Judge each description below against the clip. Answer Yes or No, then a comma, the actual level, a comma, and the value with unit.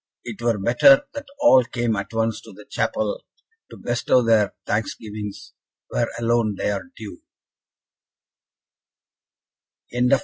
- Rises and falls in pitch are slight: Yes, narrow, 2.3 semitones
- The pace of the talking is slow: Yes, slow, 115 wpm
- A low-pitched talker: Yes, low, 115 Hz